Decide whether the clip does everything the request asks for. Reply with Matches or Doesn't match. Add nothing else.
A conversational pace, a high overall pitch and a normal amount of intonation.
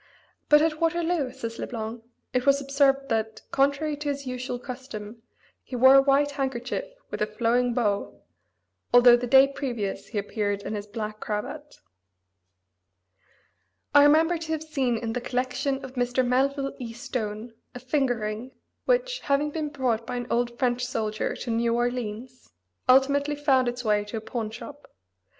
Matches